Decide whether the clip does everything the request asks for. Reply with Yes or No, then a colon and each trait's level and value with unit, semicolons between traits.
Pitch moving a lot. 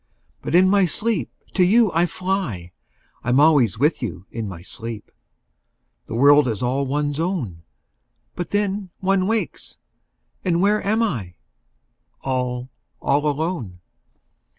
Yes: wide, 7.7 semitones